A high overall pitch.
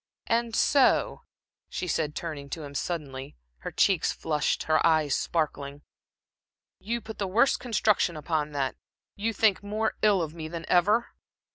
No: medium, 170 Hz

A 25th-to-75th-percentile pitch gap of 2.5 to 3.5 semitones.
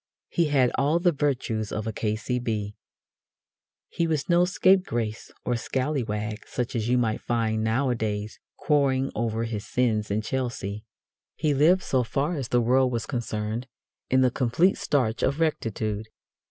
No: average, 4.1 semitones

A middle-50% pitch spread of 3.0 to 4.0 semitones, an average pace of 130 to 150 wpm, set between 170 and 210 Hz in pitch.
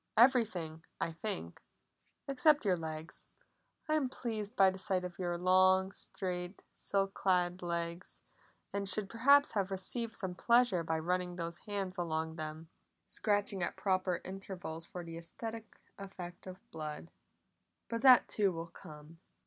Yes: average, 3.3 semitones; average, 140 wpm; medium, 185 Hz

